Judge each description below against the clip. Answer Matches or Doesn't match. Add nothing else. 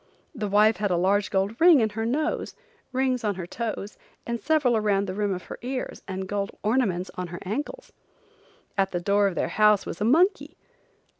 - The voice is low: Doesn't match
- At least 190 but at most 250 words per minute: Matches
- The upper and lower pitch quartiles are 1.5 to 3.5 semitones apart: Doesn't match